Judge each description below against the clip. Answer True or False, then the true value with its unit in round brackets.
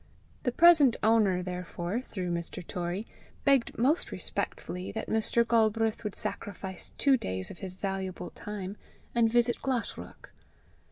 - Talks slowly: True (130 wpm)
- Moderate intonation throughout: True (4.4 semitones)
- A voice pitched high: True (210 Hz)